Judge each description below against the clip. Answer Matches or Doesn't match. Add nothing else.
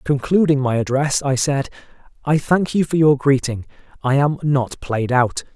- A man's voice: Matches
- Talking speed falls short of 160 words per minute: Doesn't match